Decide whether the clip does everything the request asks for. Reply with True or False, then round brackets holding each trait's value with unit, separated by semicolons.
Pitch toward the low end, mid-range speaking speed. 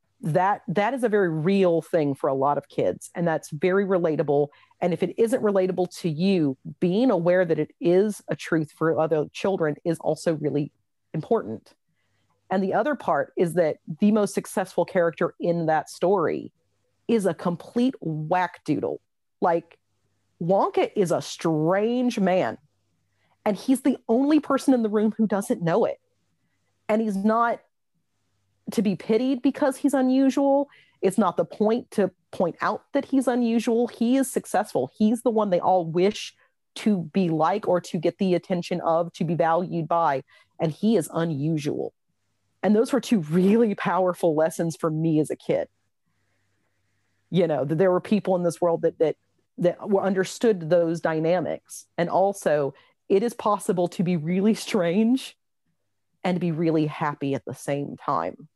False (180 Hz; 170 wpm)